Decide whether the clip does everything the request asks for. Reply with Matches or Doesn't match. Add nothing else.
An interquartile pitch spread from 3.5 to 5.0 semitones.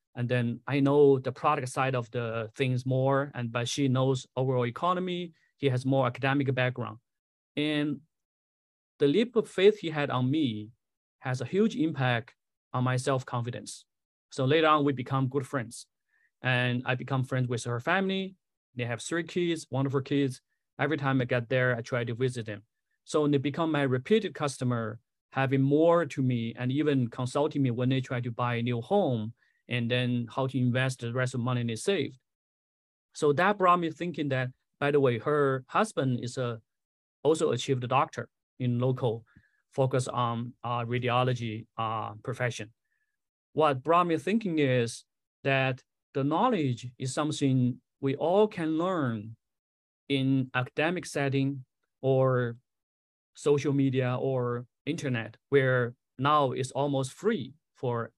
Doesn't match